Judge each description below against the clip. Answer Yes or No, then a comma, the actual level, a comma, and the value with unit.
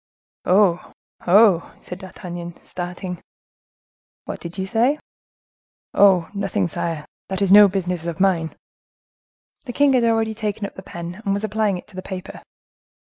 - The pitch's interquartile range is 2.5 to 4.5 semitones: Yes, average, 2.9 semitones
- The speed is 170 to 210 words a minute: No, average, 150 wpm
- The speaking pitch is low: No, high, 190 Hz